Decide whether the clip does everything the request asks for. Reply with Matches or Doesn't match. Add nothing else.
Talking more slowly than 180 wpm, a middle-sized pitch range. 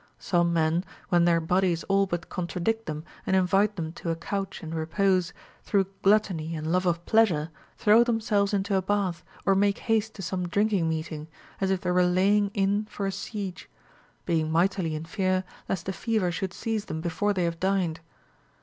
Doesn't match